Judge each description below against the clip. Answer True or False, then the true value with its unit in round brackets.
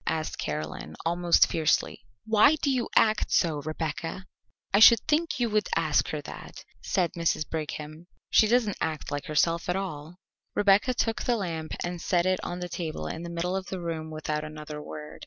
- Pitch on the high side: False (170 Hz)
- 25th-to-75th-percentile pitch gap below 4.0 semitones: False (4.5 semitones)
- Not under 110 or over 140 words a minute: False (185 wpm)